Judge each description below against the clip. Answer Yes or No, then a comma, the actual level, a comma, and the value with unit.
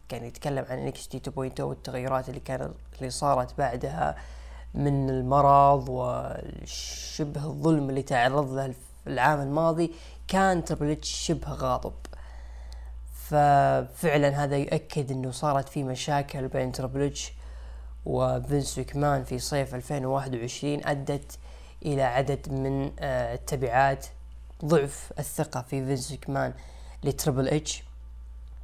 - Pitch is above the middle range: No, low, 135 Hz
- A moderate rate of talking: Yes, average, 110 wpm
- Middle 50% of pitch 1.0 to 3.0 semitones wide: No, average, 3.6 semitones